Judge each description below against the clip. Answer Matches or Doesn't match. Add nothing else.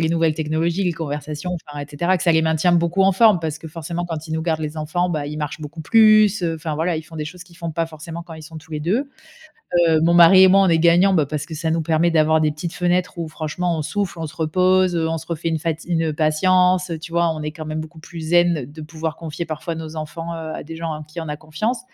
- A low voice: Doesn't match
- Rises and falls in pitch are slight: Matches